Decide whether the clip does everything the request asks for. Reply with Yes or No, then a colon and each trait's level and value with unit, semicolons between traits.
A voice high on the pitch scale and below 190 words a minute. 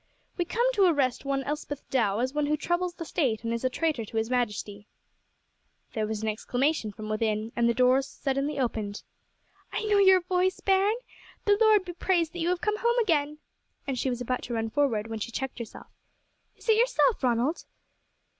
No: very high, 275 Hz; average, 200 wpm